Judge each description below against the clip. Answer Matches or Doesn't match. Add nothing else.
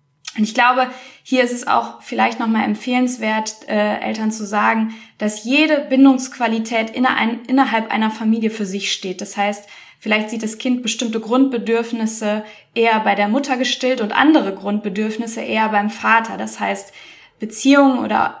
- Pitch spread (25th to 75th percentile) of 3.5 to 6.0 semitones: Doesn't match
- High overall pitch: Matches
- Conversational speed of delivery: Matches